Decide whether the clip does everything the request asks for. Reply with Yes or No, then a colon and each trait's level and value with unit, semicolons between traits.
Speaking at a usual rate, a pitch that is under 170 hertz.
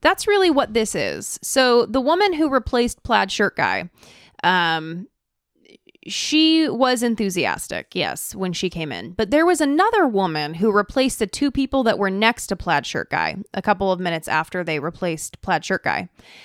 No: average, 180 wpm; high, 225 Hz